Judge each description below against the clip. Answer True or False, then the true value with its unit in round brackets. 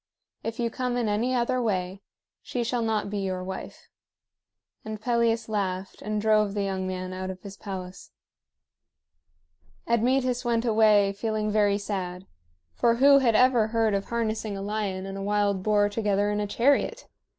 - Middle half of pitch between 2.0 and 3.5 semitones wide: True (2.9 semitones)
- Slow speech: False (165 wpm)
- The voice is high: True (210 Hz)